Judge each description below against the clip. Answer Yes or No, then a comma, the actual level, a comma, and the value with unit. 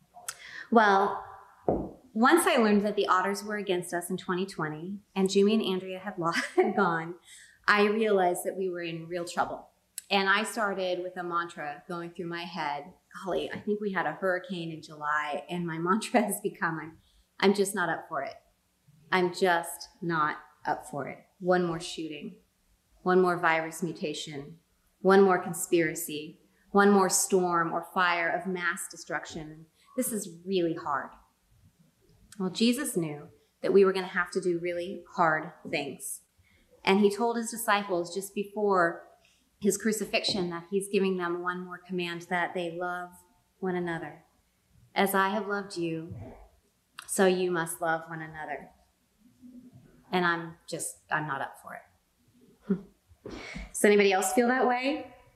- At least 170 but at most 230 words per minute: No, average, 160 wpm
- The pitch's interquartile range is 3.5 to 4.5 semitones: No, average, 2.8 semitones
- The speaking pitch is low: No, medium, 180 Hz